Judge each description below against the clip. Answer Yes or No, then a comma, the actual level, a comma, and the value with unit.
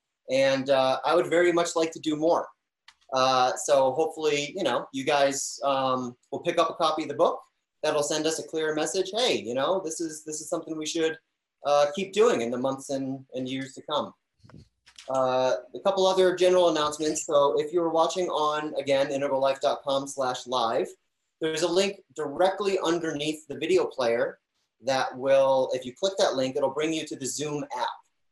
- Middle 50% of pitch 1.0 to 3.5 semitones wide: No, average, 4.0 semitones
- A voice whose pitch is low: No, medium, 155 Hz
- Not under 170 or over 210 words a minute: Yes, average, 190 wpm